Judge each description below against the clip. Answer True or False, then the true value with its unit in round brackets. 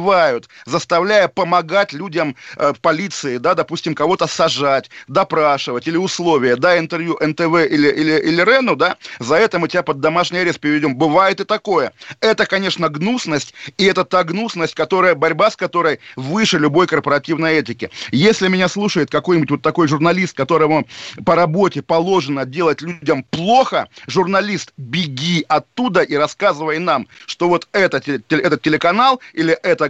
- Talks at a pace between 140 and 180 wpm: True (145 wpm)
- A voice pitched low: False (170 Hz)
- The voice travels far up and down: False (3.4 semitones)